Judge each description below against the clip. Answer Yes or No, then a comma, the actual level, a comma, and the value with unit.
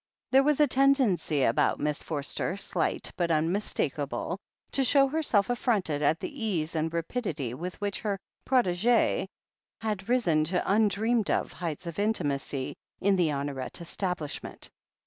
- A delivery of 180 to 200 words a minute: No, average, 145 wpm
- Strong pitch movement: Yes, wide, 6.6 semitones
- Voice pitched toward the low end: No, medium, 185 Hz